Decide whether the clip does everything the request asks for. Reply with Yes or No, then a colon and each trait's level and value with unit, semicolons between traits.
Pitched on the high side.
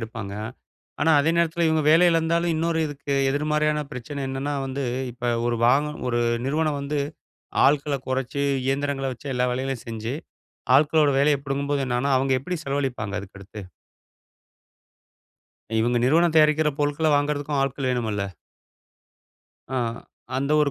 No: medium, 140 Hz